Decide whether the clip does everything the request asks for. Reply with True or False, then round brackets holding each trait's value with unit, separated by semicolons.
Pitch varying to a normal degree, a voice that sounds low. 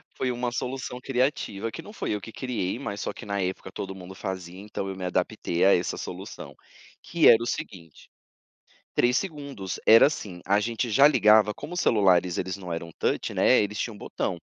True (4.8 semitones; 105 Hz)